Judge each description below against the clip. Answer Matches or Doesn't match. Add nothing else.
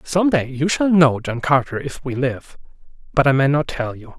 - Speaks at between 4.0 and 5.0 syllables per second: Matches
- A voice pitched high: Doesn't match